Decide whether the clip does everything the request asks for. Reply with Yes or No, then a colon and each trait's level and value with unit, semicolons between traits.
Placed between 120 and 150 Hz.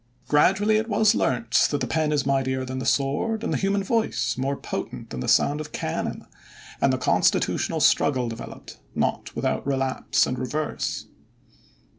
Yes: medium, 140 Hz